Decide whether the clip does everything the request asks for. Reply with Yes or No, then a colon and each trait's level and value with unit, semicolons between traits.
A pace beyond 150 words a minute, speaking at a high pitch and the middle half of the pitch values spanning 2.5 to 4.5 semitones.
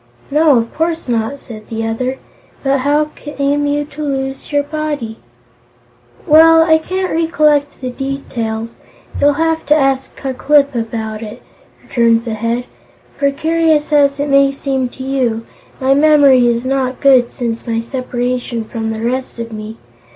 Yes: average, 160 wpm; very high, 270 Hz; average, 3.8 semitones